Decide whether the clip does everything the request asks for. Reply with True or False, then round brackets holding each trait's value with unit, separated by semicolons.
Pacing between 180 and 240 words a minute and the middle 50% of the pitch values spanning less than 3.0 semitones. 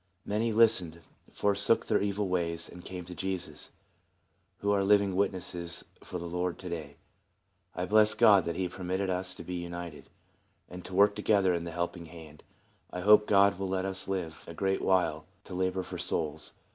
True (190 wpm; 2.4 semitones)